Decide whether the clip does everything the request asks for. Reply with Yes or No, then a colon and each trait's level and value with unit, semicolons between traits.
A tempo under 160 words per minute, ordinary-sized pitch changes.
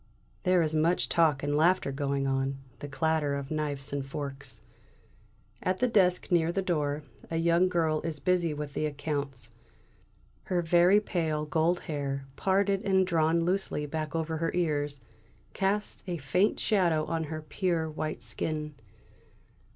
Yes: average, 150 wpm; average, 3.4 semitones